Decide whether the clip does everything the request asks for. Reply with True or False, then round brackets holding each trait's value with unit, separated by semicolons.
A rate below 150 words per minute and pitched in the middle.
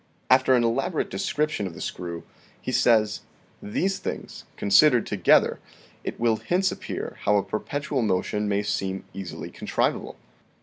False (140 wpm; 110 Hz)